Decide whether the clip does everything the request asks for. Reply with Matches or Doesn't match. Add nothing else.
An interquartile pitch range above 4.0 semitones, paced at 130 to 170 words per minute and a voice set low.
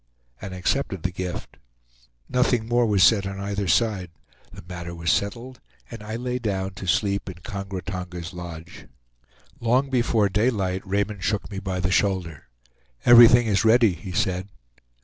Doesn't match